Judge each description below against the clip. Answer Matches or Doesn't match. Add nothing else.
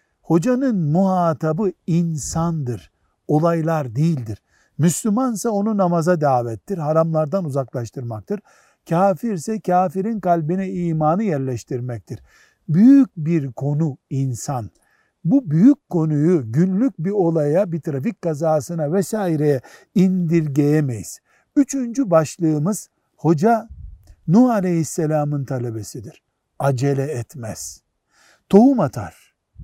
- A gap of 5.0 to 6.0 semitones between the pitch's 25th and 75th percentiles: Matches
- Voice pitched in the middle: Matches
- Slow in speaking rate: Matches